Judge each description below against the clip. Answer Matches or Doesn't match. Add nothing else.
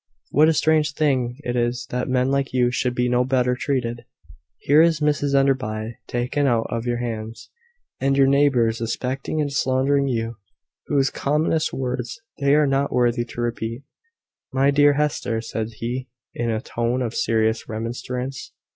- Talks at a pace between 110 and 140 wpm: Doesn't match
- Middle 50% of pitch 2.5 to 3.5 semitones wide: Matches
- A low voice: Matches